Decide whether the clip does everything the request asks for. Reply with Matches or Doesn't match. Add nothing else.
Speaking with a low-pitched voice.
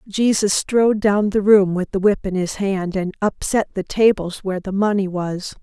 Doesn't match